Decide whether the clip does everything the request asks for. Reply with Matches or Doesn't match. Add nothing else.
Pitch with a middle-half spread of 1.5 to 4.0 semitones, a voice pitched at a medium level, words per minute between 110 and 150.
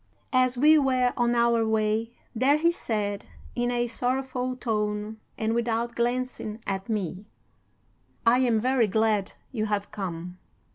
Doesn't match